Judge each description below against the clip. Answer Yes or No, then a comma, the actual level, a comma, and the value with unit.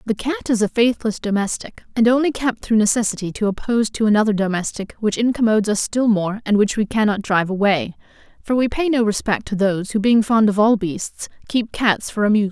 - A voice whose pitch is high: Yes, high, 215 Hz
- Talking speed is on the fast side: Yes, fast, 210 wpm